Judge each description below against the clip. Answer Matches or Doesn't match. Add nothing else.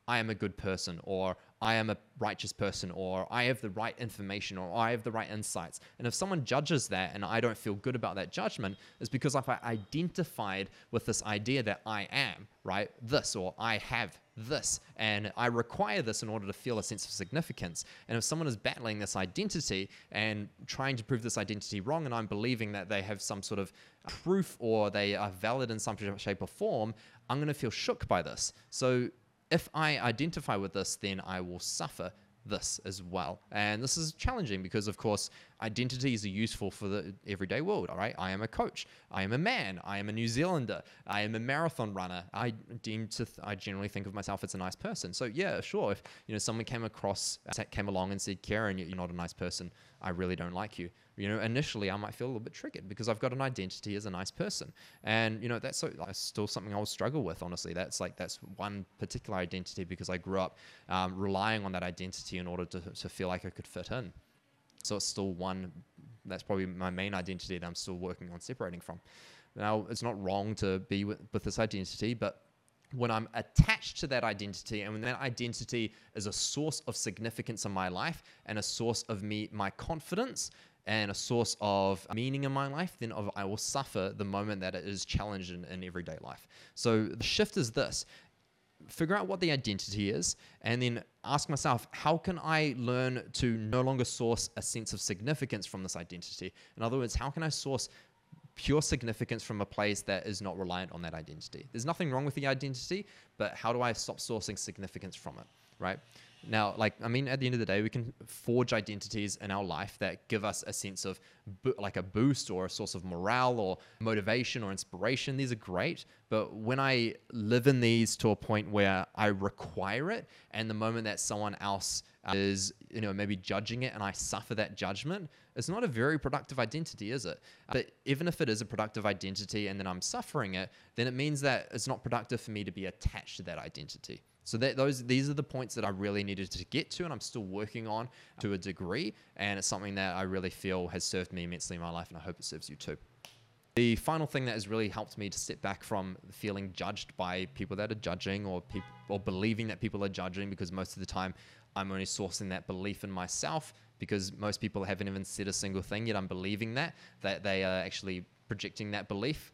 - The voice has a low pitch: Matches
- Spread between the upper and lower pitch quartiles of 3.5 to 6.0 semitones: Matches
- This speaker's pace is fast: Matches